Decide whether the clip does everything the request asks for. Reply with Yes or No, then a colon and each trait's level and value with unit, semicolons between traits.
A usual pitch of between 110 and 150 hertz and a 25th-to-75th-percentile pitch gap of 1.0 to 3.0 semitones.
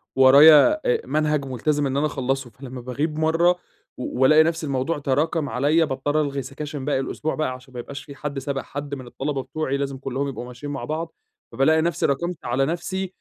Yes: medium, 140 Hz; average, 2.7 semitones